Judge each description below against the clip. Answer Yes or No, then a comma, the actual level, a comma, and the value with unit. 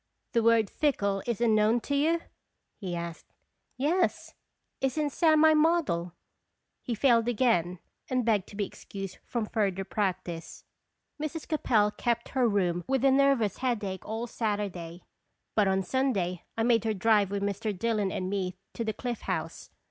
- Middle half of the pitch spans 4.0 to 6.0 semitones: Yes, average, 4.8 semitones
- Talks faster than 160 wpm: No, average, 155 wpm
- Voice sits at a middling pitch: No, high, 220 Hz